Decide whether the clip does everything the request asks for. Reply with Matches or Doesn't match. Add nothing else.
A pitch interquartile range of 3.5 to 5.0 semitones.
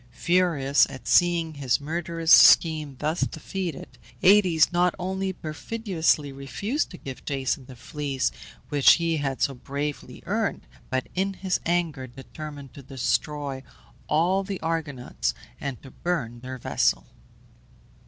Matches